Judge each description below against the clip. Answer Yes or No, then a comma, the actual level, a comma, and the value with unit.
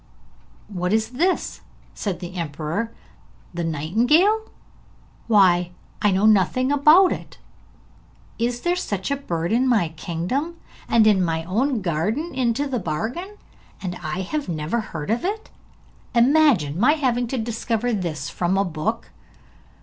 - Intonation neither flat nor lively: No, wide, 7.1 semitones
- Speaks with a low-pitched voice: No, high, 220 Hz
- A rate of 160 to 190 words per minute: No, average, 140 wpm